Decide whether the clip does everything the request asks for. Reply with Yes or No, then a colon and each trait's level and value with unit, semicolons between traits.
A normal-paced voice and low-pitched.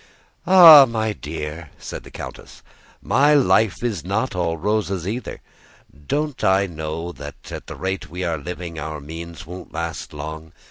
Yes: average, 155 wpm; very low, 90 Hz